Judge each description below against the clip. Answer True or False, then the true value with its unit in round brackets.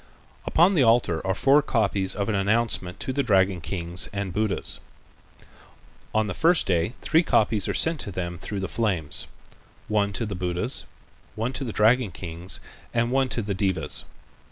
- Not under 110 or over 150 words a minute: False (175 wpm)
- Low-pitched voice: True (105 Hz)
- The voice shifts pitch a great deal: False (4.1 semitones)